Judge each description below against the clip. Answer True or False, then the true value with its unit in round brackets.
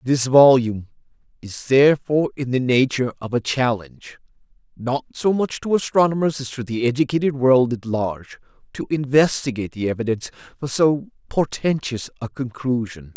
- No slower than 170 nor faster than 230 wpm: False (140 wpm)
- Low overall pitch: True (130 Hz)